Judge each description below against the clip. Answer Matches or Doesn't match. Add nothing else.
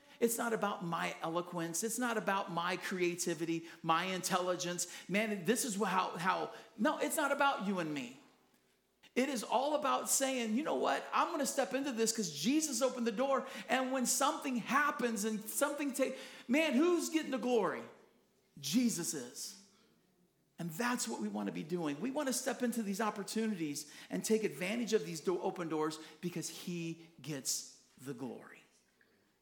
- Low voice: Doesn't match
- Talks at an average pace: Matches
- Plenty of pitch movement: Matches